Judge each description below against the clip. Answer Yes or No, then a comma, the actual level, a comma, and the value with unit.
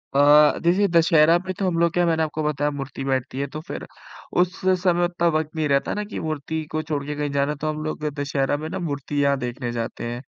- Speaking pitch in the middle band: Yes, medium, 150 Hz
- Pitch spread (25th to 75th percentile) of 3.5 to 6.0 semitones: No, average, 3.0 semitones